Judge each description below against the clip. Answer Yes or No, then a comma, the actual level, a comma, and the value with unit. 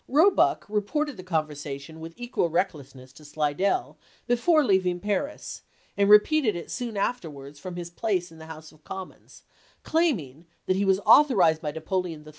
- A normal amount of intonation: No, wide, 6.0 semitones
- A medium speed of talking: Yes, average, 160 wpm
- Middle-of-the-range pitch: Yes, medium, 180 Hz